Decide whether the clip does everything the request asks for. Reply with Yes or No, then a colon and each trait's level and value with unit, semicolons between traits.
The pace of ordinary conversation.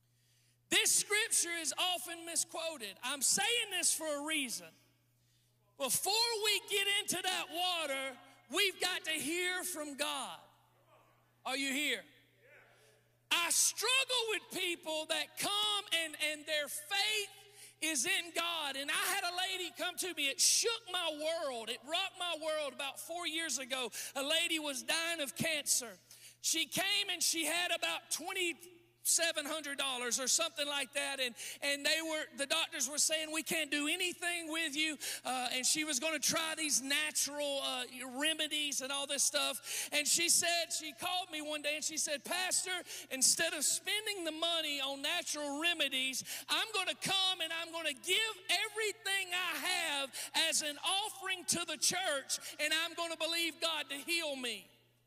Yes: average, 170 wpm